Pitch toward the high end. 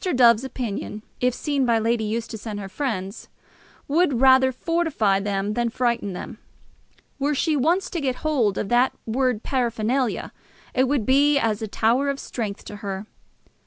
Yes: high, 240 Hz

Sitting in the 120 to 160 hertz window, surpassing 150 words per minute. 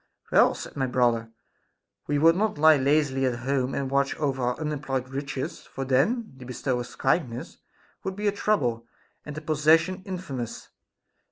Yes: medium, 140 Hz; average, 160 wpm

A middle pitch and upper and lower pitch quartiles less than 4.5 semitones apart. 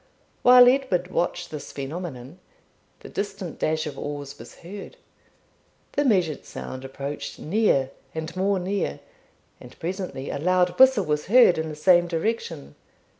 No: medium, 175 Hz; average, 5.0 semitones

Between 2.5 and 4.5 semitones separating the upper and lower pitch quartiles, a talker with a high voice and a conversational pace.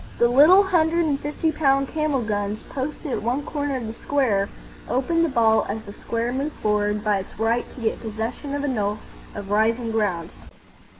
No: average, 5.1 semitones; high, 240 Hz; average, 190 wpm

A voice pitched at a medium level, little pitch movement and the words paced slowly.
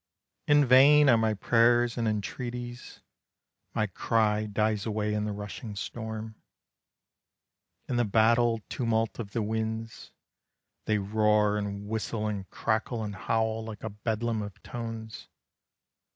No: low, 110 Hz; narrow, 1.7 semitones; slow, 130 wpm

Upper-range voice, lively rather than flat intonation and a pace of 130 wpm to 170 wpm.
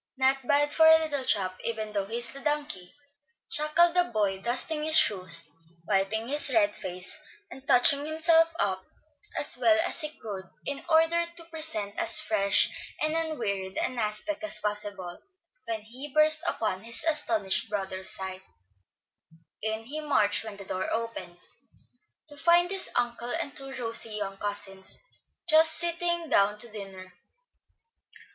Yes: high, 230 Hz; wide, 7.3 semitones; average, 150 wpm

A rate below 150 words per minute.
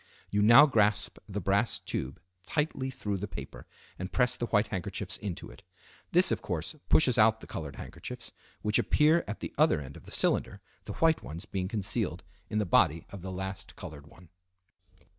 No: average, 185 wpm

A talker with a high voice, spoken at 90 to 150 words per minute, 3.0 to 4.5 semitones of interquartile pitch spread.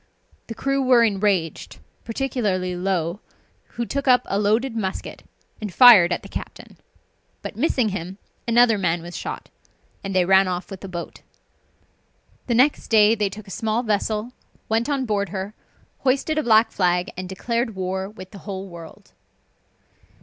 No: high, 205 Hz; average, 160 wpm; average, 3.9 semitones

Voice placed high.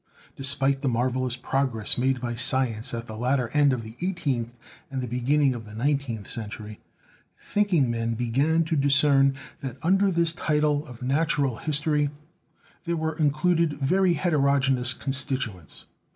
No: low, 135 Hz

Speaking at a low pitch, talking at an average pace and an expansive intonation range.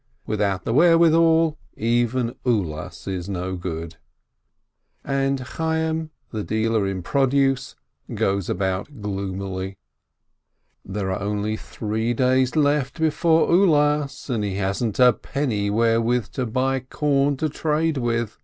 No: low, 120 Hz; slow, 120 wpm; wide, 6.1 semitones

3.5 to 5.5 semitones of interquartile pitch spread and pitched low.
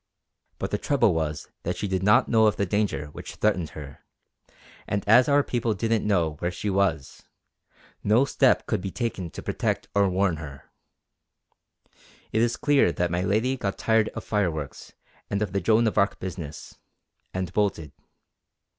Yes: average, 4.1 semitones; low, 100 Hz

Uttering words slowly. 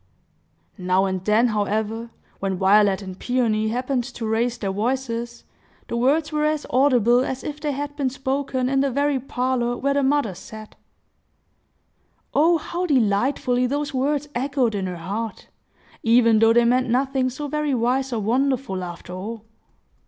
No: average, 160 wpm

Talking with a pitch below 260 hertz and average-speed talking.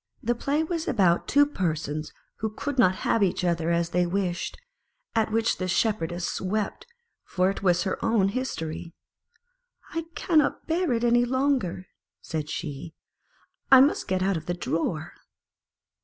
Yes: high, 190 Hz; average, 155 wpm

